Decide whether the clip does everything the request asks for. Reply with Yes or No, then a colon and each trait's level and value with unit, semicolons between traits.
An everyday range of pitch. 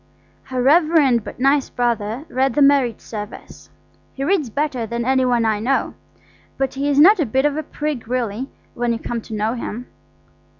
Yes: average, 3.4 semitones